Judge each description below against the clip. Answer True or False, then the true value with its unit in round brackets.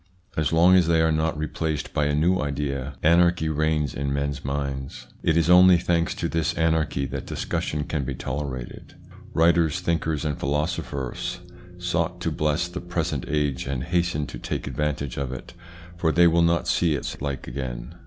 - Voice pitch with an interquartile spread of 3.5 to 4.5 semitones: False (3.1 semitones)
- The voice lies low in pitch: True (75 Hz)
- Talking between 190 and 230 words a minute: False (175 wpm)